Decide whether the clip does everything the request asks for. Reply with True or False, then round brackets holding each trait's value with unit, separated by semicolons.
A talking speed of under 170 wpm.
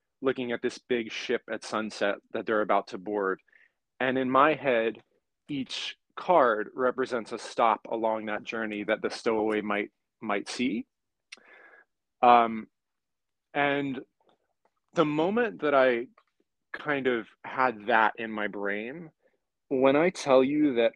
True (135 wpm)